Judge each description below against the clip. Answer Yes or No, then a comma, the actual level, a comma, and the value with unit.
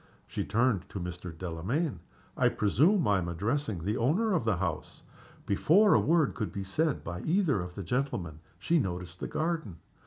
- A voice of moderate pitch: No, low, 105 Hz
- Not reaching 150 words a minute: No, average, 180 wpm